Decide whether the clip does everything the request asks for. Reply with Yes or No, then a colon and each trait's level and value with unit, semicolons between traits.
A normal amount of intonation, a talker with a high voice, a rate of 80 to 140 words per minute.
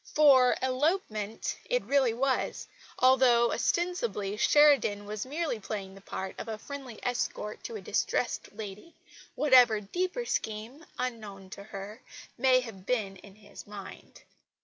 Yes: average, 4.8 semitones; high, 235 Hz; slow, 135 wpm